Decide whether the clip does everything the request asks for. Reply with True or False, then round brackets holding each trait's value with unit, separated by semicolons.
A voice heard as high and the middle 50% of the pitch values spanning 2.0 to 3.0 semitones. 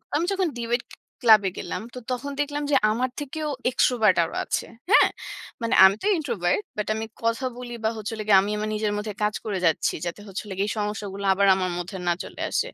False (215 Hz; 3.8 semitones)